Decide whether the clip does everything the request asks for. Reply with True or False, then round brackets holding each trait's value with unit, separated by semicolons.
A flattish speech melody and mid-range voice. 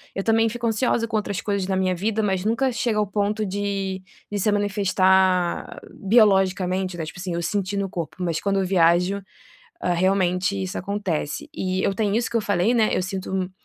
False (2.1 semitones; 195 Hz)